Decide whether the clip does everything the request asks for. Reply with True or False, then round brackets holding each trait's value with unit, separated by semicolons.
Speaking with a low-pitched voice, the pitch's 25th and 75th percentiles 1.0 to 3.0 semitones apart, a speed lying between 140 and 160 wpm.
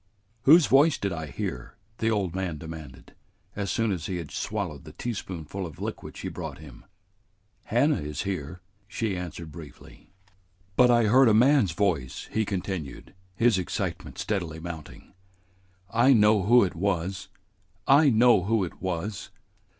False (95 Hz; 5.3 semitones; 150 wpm)